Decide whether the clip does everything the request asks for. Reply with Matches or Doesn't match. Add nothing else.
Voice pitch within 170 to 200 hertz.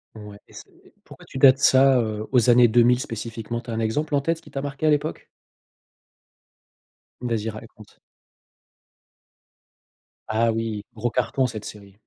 Doesn't match